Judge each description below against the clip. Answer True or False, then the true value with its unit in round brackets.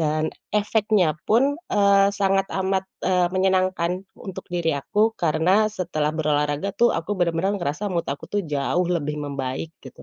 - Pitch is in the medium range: True (180 Hz)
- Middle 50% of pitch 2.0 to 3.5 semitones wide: False (4.2 semitones)